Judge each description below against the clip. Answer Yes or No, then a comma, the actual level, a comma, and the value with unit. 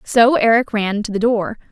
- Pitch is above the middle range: Yes, high, 220 Hz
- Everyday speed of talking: No, fast, 210 wpm